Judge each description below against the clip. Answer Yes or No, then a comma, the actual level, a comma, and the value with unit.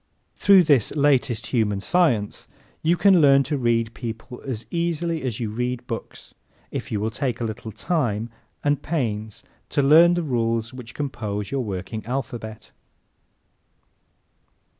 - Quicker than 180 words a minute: No, average, 140 wpm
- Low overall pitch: Yes, low, 125 Hz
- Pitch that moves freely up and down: No, average, 4.8 semitones